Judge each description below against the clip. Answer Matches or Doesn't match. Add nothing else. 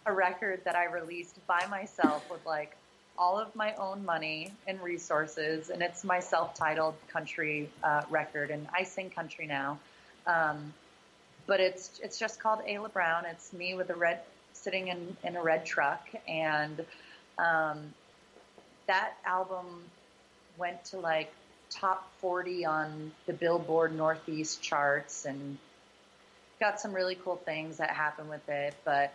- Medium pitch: Matches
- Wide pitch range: Doesn't match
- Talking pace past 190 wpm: Doesn't match